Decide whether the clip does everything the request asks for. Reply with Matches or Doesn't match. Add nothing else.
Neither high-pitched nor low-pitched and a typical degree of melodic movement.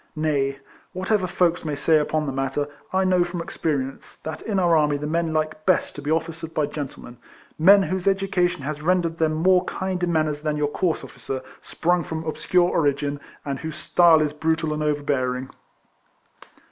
Matches